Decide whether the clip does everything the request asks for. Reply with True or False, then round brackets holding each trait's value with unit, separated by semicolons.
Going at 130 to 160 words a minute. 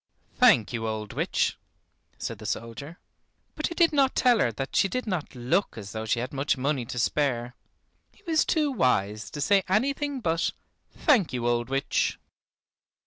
False (175 wpm)